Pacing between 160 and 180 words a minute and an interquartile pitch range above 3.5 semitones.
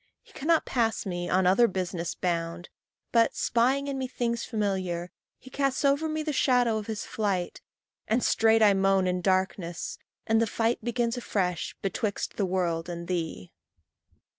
Yes: average, 165 wpm; average, 4.9 semitones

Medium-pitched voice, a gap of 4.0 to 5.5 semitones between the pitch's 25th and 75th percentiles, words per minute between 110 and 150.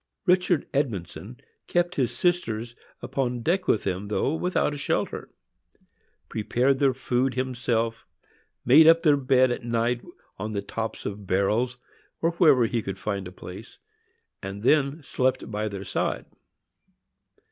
No: low, 125 Hz; average, 4.8 semitones; average, 140 wpm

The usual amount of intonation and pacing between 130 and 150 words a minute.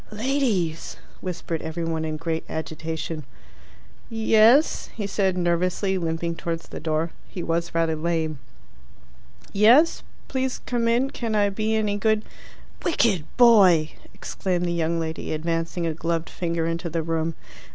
Yes: average, 4.6 semitones; average, 140 wpm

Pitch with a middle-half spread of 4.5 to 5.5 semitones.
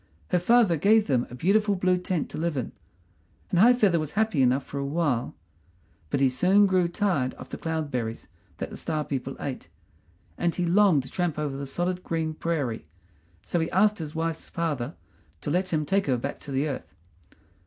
Yes: average, 4.8 semitones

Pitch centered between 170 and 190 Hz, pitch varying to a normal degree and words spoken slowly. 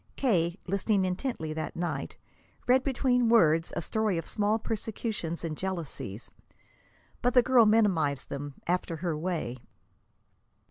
No: medium, 185 Hz; wide, 5.7 semitones; slow, 130 wpm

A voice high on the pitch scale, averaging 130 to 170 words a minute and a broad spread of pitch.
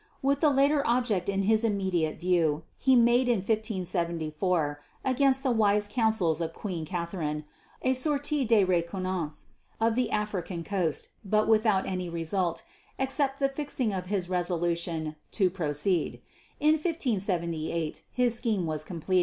Yes: high, 195 Hz; average, 140 wpm; wide, 5.8 semitones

